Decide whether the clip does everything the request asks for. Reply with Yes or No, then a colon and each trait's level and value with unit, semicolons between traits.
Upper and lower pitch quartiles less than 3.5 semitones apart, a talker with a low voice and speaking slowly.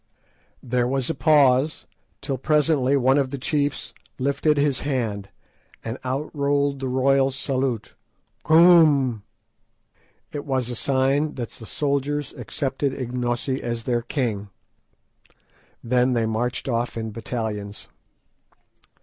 Yes: average, 2.8 semitones; low, 130 Hz; slow, 120 wpm